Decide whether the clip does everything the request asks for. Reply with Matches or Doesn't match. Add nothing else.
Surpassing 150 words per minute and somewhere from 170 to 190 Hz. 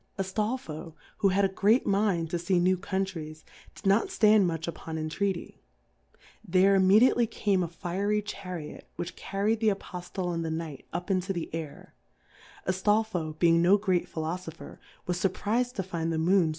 Matches